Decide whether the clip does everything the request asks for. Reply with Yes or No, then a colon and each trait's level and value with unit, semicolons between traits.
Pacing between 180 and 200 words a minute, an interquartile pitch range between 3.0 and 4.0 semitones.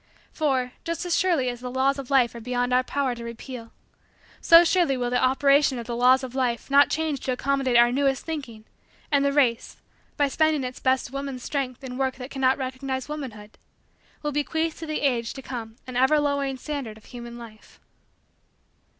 No: average, 195 wpm; narrow, 2.4 semitones